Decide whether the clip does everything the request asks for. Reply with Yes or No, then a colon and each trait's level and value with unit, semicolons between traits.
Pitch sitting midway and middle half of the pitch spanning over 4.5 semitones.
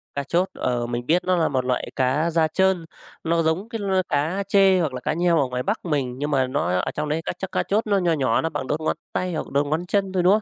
Yes: medium, 160 Hz; average, 4.9 semitones